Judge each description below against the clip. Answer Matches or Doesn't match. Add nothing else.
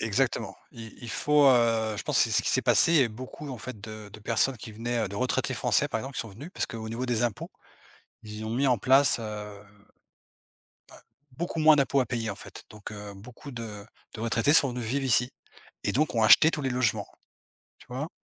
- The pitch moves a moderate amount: Matches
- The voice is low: Matches